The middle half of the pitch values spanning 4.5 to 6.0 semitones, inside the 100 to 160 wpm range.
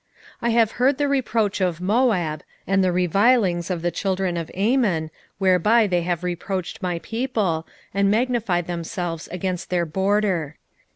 No: average, 4.0 semitones; average, 155 wpm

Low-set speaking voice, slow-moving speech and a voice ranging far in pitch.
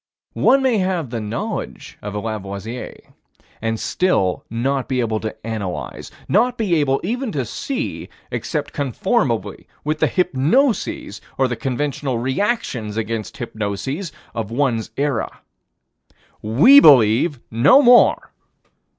Yes: low, 130 Hz; slow, 125 wpm; wide, 8.4 semitones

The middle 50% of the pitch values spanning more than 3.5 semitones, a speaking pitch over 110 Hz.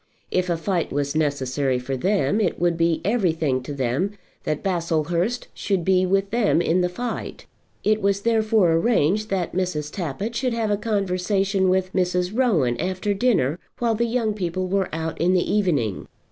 Yes: average, 4.2 semitones; medium, 185 Hz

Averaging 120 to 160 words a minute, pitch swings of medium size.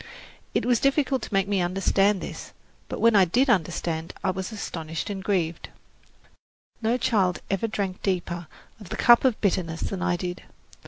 No: average, 170 wpm; average, 3.8 semitones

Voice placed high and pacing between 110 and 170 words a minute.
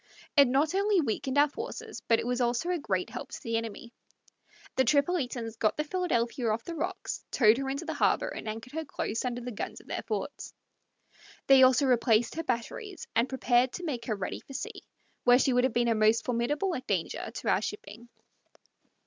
No: very high, 250 Hz; average, 200 wpm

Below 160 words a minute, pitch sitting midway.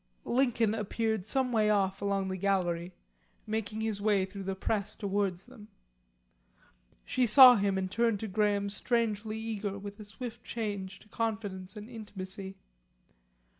No: average, 145 wpm; high, 205 Hz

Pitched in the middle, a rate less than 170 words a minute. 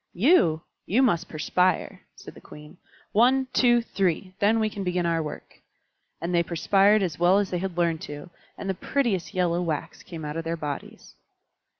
No: medium, 180 Hz; average, 185 wpm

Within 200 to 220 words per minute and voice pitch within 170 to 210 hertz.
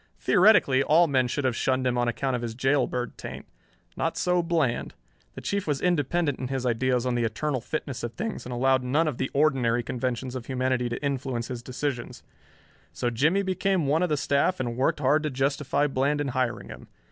No: fast, 205 wpm; low, 135 Hz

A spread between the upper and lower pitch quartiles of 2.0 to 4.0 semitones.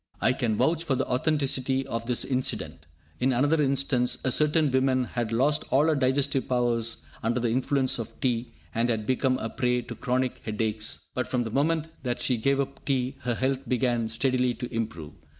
Yes: narrow, 2.4 semitones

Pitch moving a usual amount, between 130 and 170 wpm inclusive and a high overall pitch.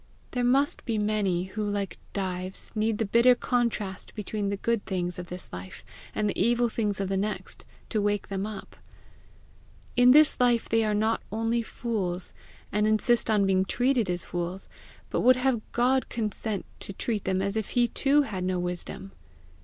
No: average, 3.5 semitones; average, 180 wpm; high, 210 Hz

